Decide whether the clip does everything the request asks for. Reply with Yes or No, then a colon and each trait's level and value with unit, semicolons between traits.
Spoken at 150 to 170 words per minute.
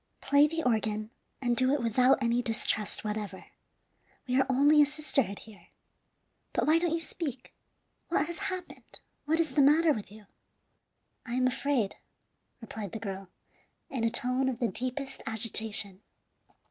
Yes: average, 155 wpm